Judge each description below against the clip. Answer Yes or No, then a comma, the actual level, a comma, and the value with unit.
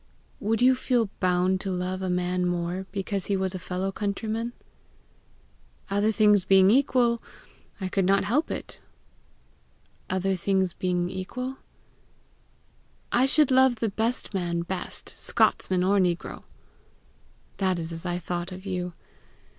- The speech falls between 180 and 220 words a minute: No, average, 145 wpm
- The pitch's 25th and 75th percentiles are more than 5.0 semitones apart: No, average, 3.2 semitones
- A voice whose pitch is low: No, high, 190 Hz